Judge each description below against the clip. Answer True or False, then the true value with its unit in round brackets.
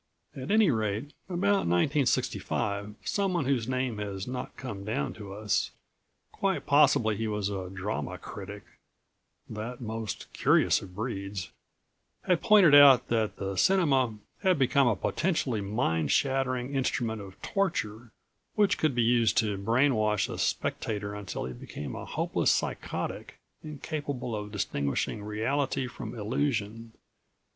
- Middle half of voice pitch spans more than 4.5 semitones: True (5.1 semitones)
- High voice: False (115 Hz)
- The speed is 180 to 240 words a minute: False (135 wpm)